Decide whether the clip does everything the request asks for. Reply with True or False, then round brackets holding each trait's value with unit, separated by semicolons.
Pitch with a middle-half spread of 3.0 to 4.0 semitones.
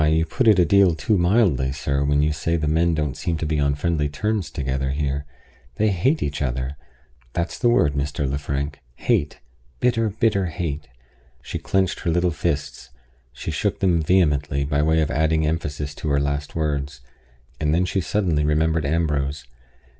True (3.3 semitones)